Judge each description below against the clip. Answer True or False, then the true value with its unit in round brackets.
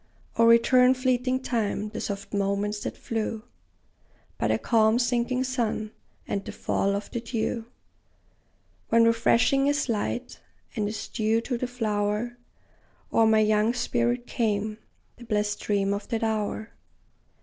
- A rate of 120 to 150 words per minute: True (140 wpm)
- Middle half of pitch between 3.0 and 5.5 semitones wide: False (2.4 semitones)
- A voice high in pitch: True (225 Hz)